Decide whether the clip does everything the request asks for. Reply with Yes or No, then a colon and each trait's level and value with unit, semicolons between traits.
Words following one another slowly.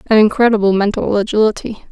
Yes: slow, 125 wpm